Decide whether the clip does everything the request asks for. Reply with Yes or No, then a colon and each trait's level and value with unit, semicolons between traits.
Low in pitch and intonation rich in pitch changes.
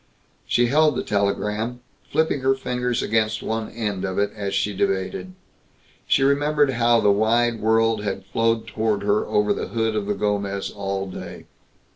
No: low, 110 Hz; average, 2.9 semitones